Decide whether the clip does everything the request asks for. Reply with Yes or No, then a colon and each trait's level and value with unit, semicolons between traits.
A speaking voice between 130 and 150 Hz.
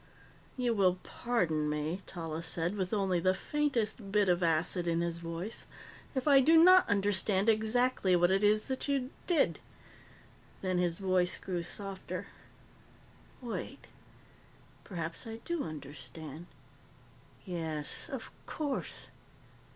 No: high, 190 Hz